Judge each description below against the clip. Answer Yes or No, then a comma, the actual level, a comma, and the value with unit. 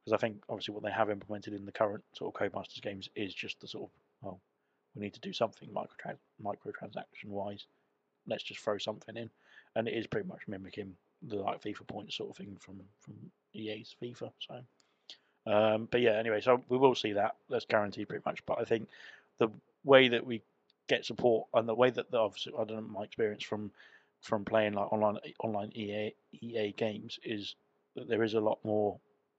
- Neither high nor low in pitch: No, low, 105 Hz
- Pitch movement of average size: No, narrow, 1.5 semitones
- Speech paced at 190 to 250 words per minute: Yes, fast, 205 wpm